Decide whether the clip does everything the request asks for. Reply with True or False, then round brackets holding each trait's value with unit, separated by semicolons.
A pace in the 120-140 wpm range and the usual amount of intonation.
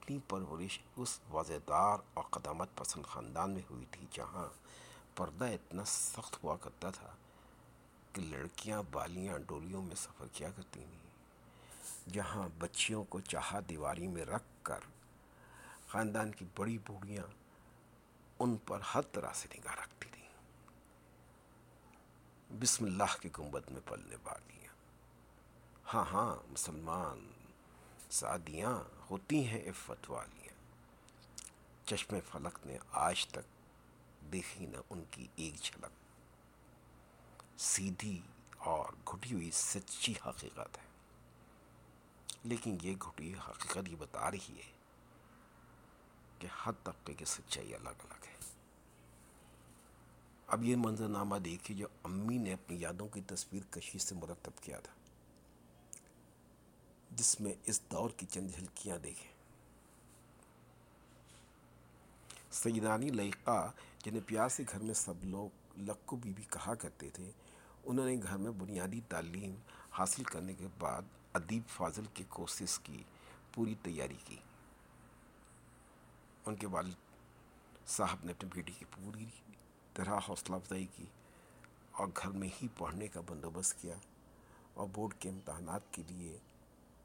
False (125 wpm; 5.7 semitones)